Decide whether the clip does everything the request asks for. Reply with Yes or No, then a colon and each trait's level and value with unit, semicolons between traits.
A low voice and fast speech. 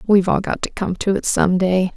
No: high, 190 Hz; fast, 275 wpm